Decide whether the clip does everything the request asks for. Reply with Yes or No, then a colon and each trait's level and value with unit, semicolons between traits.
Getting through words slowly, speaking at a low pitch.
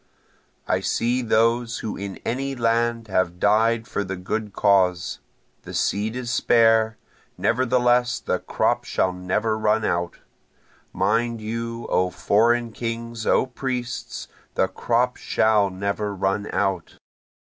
Yes: slow, 125 wpm; low, 110 Hz